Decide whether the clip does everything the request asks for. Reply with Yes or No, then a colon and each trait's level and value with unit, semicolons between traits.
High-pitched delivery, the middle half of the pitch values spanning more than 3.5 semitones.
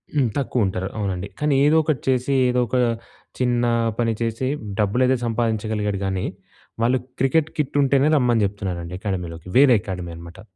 No: low, 115 Hz; average, 5.2 semitones